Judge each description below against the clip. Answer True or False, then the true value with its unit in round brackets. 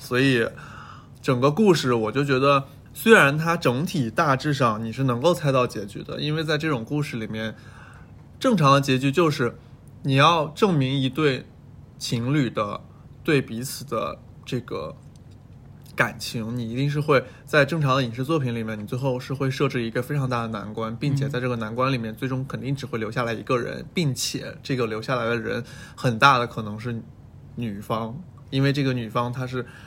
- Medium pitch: False (130 Hz)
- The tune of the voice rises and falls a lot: False (2.8 semitones)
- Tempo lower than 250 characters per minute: False (275 characters per minute)